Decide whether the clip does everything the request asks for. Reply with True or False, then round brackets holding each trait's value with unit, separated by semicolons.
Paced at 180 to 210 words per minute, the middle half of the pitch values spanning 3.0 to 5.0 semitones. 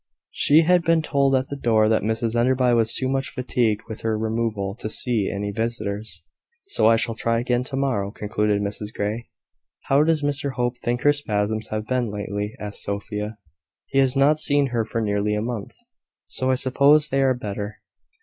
True (190 wpm; 4.0 semitones)